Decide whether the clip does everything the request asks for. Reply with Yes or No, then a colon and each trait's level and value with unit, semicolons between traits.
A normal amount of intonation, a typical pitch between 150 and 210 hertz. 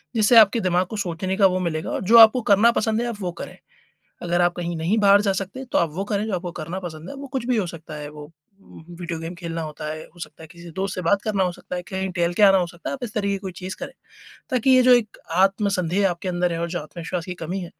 Yes: average, 3.2 semitones; medium, 185 Hz